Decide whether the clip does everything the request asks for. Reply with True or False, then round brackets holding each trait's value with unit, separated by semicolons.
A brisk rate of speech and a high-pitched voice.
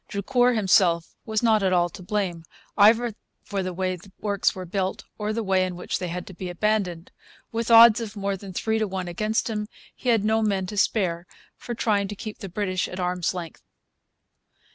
True (210 wpm; 200 Hz)